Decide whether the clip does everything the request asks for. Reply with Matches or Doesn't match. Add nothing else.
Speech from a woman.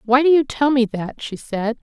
Matches